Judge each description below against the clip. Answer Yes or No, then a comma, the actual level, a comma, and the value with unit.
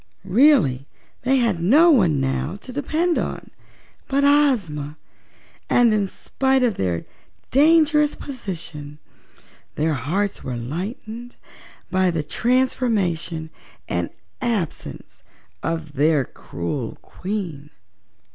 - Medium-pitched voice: No, high, 195 Hz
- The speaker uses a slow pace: Yes, slow, 100 wpm